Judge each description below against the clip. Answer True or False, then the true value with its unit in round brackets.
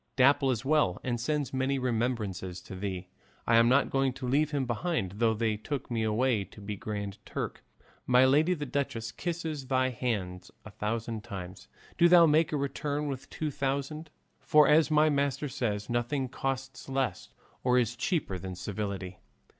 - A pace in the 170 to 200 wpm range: True (175 wpm)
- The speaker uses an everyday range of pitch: True (4.9 semitones)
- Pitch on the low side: True (125 Hz)